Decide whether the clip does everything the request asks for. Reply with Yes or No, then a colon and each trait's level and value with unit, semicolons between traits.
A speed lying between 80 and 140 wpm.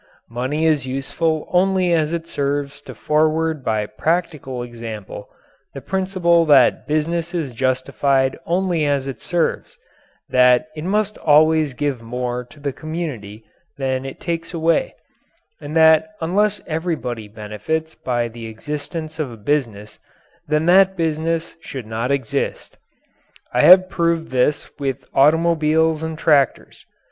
Yes: slow, 135 wpm